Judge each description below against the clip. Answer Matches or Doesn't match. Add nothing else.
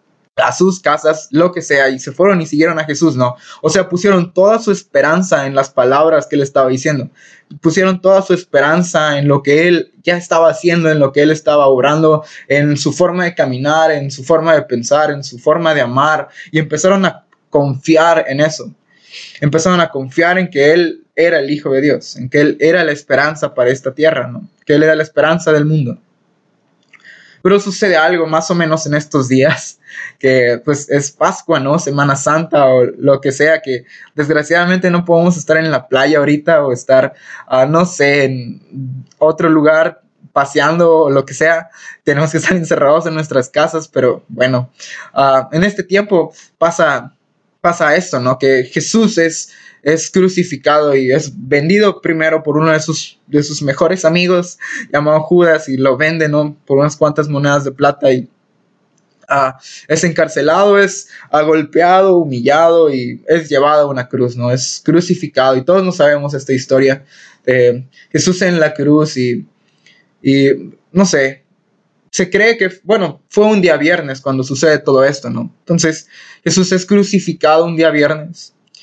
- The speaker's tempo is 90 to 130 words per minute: Doesn't match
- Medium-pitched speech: Matches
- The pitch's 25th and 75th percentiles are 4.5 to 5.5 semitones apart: Doesn't match